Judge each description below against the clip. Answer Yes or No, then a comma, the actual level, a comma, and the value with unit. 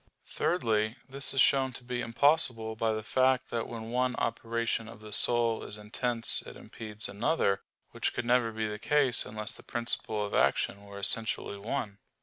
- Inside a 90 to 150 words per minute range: No, average, 175 wpm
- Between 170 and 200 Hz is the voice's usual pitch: No, low, 115 Hz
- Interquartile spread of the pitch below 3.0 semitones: Yes, narrow, 2.6 semitones